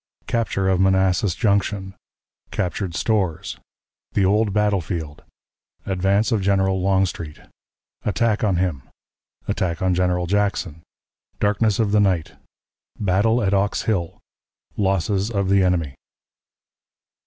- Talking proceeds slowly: Yes, slow, 115 wpm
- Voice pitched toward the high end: No, very low, 95 Hz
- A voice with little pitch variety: Yes, narrow, 2.2 semitones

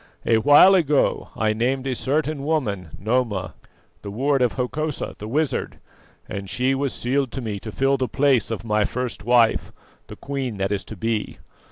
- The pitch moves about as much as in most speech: Yes, average, 4.1 semitones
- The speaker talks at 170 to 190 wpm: Yes, average, 180 wpm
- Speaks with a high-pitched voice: No, low, 125 Hz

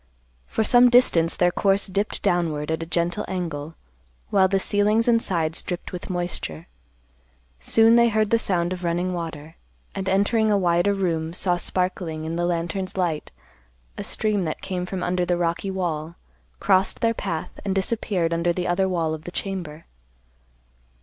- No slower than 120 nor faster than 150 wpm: No, average, 170 wpm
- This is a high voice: No, medium, 180 Hz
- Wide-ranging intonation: No, average, 2.8 semitones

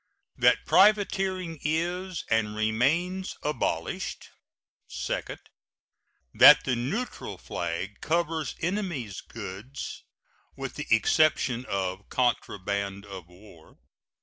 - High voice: No, low, 125 Hz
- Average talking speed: No, slow, 90 wpm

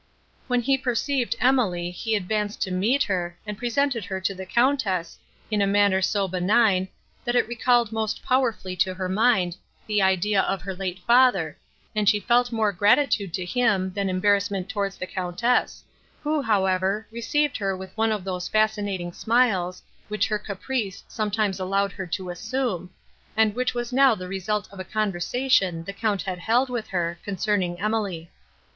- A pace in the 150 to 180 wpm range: Yes, average, 170 wpm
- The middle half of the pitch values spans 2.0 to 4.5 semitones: Yes, average, 3.9 semitones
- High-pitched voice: Yes, high, 205 Hz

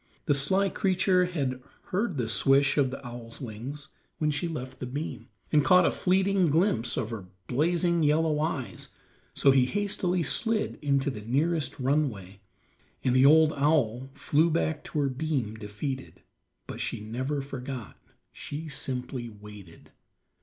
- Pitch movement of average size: Yes, average, 4.4 semitones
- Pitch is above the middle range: No, medium, 140 Hz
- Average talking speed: Yes, average, 145 wpm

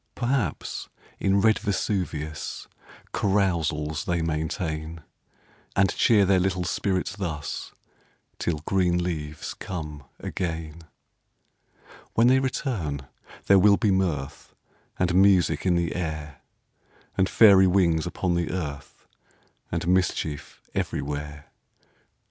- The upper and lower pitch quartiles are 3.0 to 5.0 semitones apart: Yes, average, 3.7 semitones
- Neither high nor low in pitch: No, very low, 90 Hz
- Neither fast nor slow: No, slow, 105 wpm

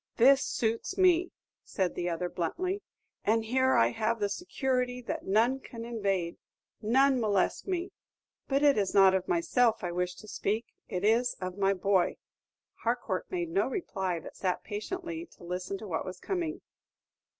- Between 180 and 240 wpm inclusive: No, average, 165 wpm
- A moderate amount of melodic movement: No, wide, 6.6 semitones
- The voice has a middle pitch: No, high, 225 Hz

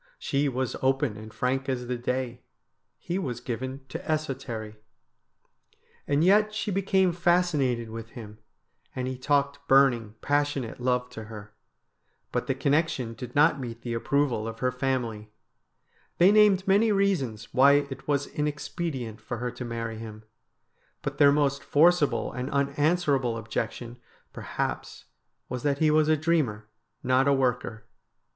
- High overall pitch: No, low, 130 Hz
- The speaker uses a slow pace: No, average, 150 wpm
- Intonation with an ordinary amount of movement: Yes, average, 3.9 semitones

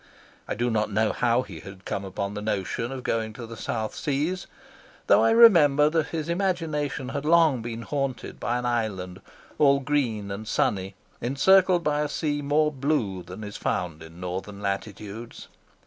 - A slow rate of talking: No, average, 175 wpm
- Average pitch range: No, wide, 6.3 semitones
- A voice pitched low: Yes, low, 120 Hz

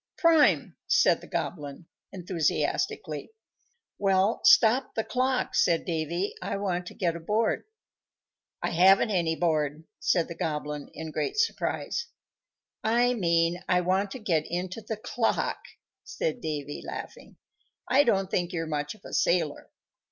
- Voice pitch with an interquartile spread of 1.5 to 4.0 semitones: No, average, 5.1 semitones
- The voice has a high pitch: No, medium, 180 Hz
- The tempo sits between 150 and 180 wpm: No, slow, 135 wpm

